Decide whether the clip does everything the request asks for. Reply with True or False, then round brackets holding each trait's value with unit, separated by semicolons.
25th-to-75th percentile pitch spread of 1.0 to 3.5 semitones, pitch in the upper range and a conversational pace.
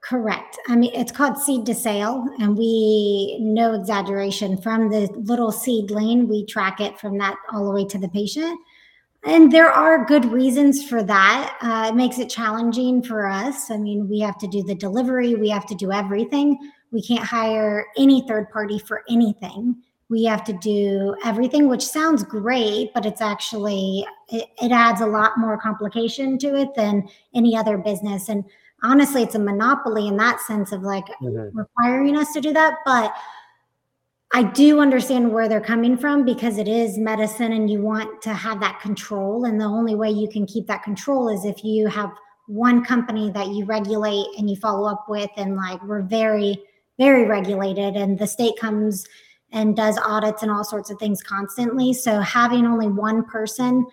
True (2.8 semitones; 220 Hz; 185 wpm)